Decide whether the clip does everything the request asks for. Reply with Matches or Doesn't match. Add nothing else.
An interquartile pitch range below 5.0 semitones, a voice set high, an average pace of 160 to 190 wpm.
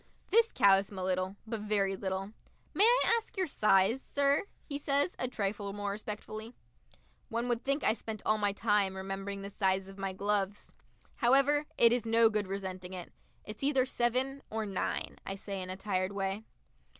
Matches